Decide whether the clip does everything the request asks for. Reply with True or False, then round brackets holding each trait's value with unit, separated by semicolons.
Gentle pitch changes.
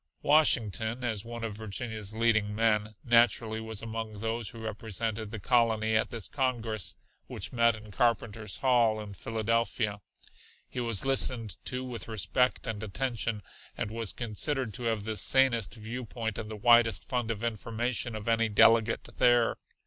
True (1.6 semitones)